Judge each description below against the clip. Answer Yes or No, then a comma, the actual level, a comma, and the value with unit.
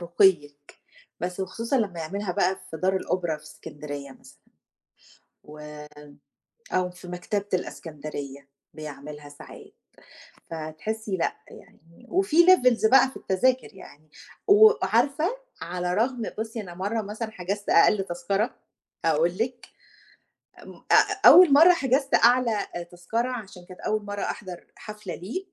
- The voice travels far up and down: Yes, wide, 5.7 semitones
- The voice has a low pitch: No, high, 190 Hz